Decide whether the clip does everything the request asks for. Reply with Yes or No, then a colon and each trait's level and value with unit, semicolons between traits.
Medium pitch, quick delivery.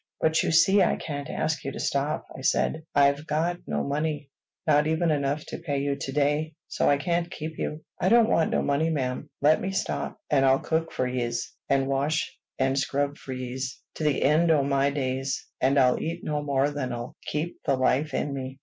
Yes: medium, 145 Hz; fast, 210 wpm